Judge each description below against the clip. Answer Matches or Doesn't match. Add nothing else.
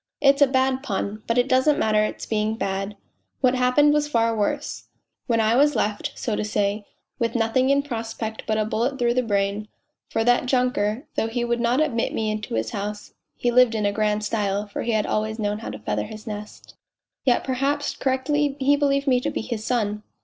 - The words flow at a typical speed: Doesn't match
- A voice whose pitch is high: Matches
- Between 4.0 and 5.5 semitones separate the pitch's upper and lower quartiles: Doesn't match